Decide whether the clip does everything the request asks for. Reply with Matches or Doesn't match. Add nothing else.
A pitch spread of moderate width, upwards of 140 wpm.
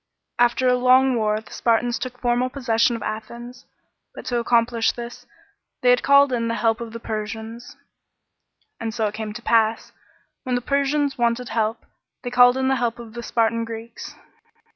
Doesn't match